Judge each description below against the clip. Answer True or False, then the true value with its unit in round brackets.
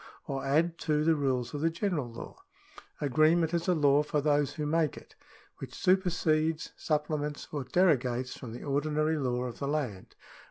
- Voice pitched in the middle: True (150 Hz)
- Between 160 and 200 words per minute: True (170 wpm)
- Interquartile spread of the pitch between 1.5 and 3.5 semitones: True (2.8 semitones)